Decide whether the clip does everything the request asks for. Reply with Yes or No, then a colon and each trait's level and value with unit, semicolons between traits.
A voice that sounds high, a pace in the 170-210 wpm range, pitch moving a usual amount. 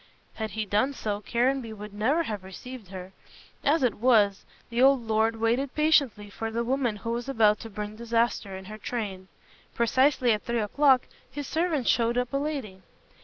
Yes: high, 230 Hz; average, 180 wpm; average, 3.8 semitones